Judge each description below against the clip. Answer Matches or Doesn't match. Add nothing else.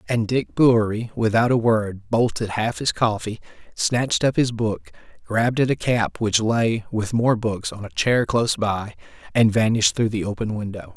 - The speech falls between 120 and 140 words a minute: Doesn't match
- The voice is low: Matches